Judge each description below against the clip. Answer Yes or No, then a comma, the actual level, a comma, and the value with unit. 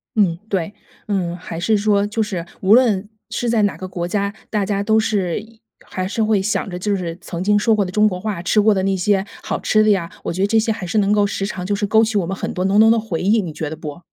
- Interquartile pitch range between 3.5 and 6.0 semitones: No, average, 2.7 semitones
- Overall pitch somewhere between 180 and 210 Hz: Yes, high, 200 Hz